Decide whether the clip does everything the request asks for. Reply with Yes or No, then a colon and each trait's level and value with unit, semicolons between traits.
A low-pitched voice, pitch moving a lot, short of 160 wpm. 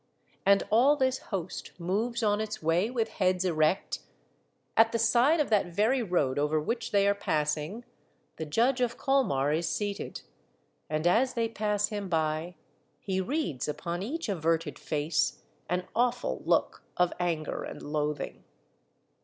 No: high, 195 Hz; wide, 6.3 semitones; average, 150 wpm